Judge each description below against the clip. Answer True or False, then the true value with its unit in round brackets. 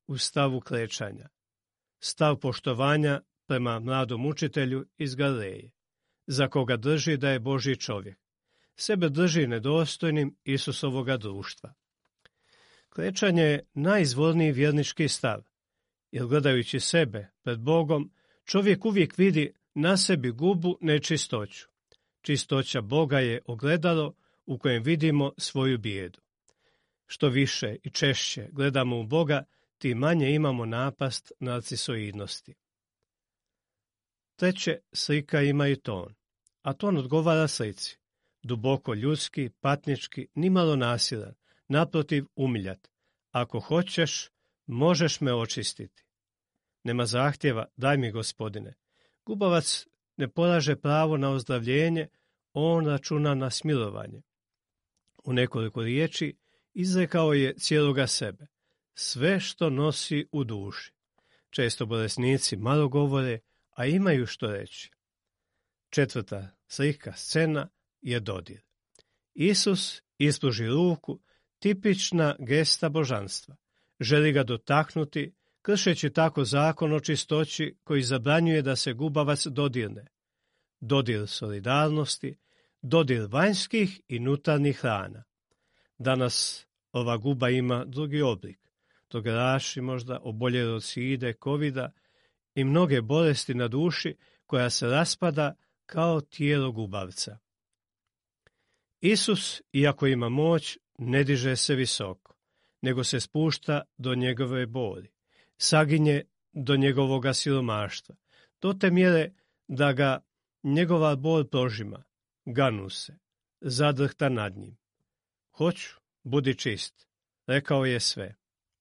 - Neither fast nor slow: False (105 wpm)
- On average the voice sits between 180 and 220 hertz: False (140 Hz)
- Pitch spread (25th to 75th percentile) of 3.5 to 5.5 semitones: True (4.2 semitones)